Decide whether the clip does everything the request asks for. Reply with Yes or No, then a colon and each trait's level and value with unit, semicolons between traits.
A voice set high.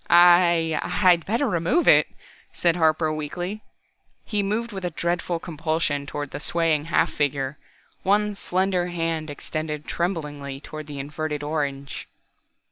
No: medium, 165 Hz